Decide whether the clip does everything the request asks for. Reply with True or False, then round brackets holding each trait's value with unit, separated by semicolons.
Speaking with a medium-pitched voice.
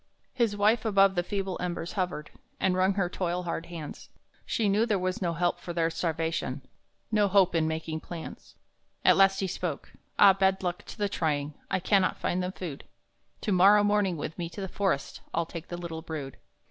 True (180 Hz)